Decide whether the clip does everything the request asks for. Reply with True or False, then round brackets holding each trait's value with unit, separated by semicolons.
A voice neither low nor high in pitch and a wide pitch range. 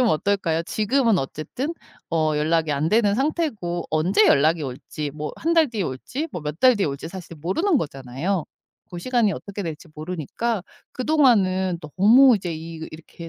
True (180 Hz; 6.7 semitones)